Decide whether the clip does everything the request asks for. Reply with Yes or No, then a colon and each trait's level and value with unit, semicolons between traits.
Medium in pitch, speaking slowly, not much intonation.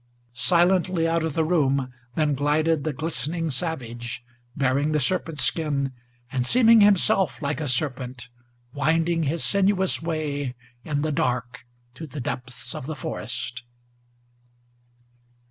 No: medium, 150 Hz; slow, 130 wpm; average, 4.0 semitones